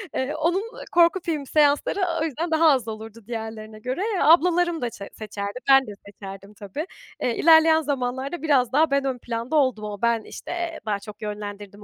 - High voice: Yes, very high, 255 Hz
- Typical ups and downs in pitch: No, wide, 6.6 semitones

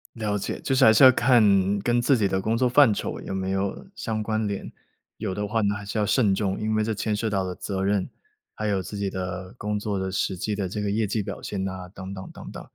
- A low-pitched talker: Yes, low, 105 Hz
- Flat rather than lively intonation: Yes, narrow, 2.2 semitones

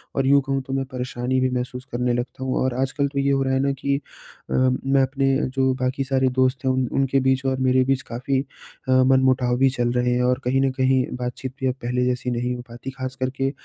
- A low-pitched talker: Yes, low, 130 Hz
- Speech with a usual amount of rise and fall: No, narrow, 1.1 semitones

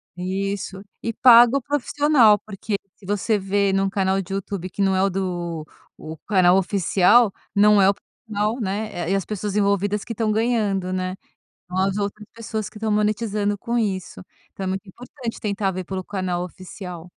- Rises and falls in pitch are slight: Yes, narrow, 2.2 semitones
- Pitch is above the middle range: Yes, high, 200 Hz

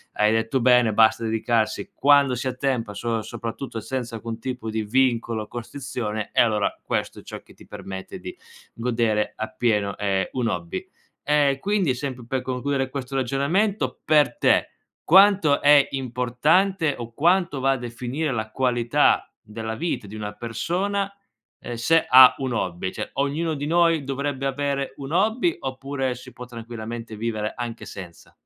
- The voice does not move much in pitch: No, average, 3.9 semitones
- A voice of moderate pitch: No, low, 125 Hz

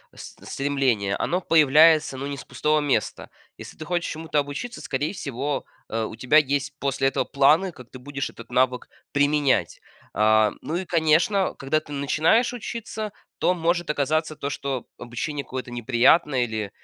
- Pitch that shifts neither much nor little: Yes, average, 3.5 semitones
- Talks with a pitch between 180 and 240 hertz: No, medium, 145 Hz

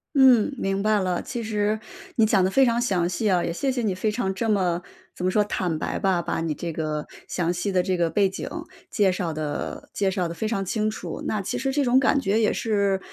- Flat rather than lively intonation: No, average, 3.6 semitones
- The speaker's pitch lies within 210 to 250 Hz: No, high, 195 Hz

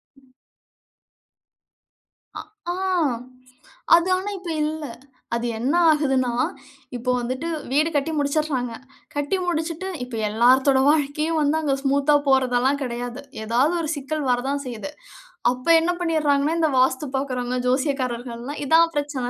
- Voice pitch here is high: Yes, very high, 280 Hz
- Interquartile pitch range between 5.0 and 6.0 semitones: No, average, 3.4 semitones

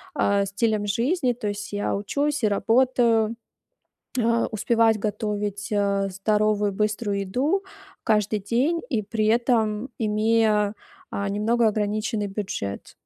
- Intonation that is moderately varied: No, narrow, 2.2 semitones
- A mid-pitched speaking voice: No, high, 215 Hz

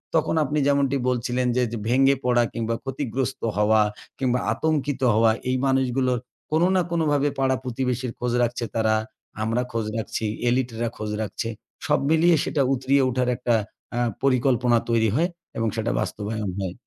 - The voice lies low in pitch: Yes, low, 125 Hz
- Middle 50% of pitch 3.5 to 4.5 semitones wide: No, average, 2.8 semitones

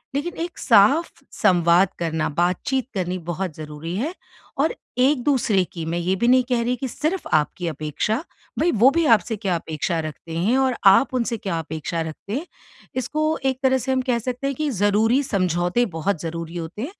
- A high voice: Yes, high, 205 Hz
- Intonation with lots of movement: Yes, wide, 7.4 semitones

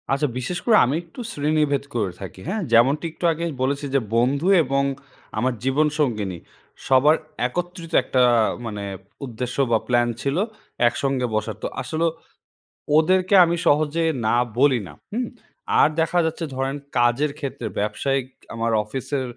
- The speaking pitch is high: No, low, 135 Hz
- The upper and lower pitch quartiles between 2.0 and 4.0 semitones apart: No, average, 4.4 semitones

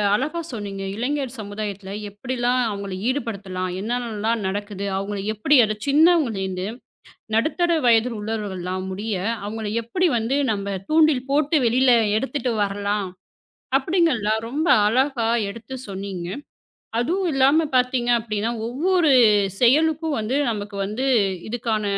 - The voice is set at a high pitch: Yes, high, 230 Hz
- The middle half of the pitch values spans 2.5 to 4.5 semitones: No, average, 5.0 semitones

